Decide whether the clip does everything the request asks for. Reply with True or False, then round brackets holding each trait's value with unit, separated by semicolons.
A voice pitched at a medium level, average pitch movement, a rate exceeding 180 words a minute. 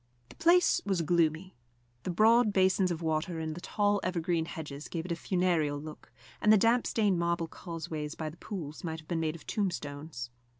True (170 Hz; 3.3 semitones; 190 wpm)